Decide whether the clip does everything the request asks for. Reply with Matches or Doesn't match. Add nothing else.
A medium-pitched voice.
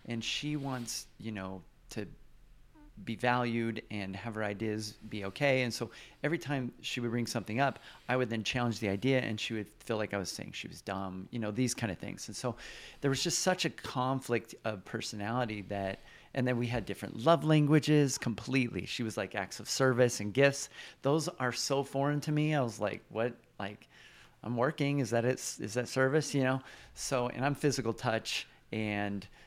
Doesn't match